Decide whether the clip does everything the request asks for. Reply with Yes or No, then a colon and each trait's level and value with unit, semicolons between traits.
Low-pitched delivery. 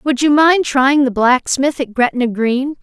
No: very high, 265 Hz